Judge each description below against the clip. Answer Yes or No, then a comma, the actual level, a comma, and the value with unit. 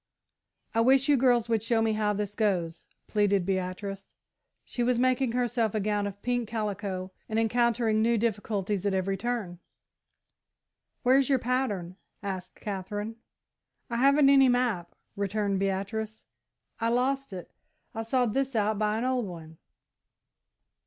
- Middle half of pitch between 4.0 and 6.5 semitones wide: No, average, 3.6 semitones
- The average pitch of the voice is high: Yes, high, 220 Hz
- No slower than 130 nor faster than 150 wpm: Yes, average, 145 wpm